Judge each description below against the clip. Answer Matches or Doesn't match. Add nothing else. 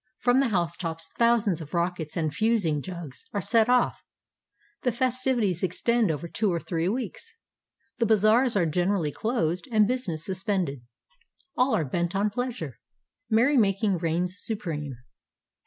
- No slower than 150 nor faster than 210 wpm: Doesn't match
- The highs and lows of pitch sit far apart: Matches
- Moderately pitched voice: Doesn't match